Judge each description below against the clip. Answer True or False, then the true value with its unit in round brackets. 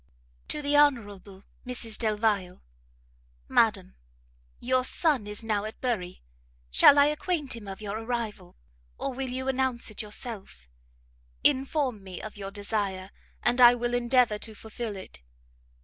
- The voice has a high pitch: True (230 Hz)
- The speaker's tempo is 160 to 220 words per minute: False (140 wpm)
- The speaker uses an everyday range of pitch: True (3.8 semitones)